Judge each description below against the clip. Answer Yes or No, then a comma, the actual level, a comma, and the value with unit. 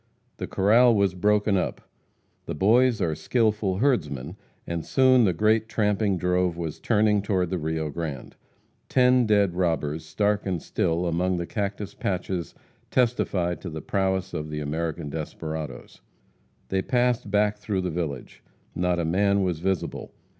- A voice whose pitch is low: Yes, very low, 95 Hz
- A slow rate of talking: No, average, 150 wpm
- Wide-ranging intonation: No, average, 4.0 semitones